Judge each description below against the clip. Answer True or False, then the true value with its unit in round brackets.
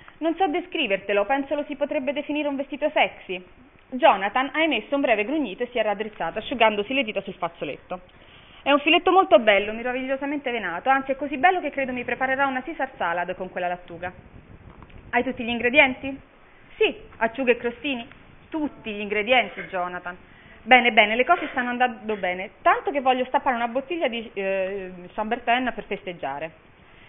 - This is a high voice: True (245 Hz)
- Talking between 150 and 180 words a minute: True (170 wpm)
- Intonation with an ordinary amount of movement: False (5.9 semitones)